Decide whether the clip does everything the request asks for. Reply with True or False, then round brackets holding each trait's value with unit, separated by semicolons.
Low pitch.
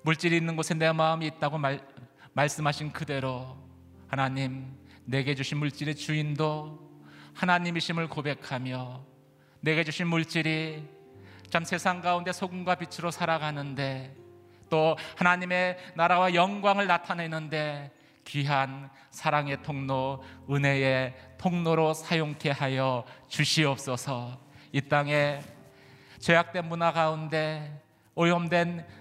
False (150 Hz)